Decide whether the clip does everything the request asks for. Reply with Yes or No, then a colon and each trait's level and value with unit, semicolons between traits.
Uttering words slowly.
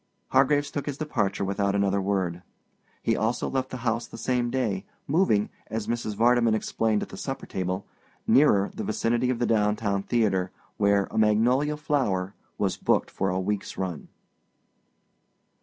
No: average, 155 wpm